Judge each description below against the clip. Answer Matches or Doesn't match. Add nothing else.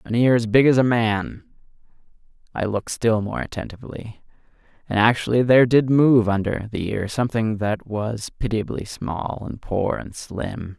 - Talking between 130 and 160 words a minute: Matches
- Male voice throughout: Matches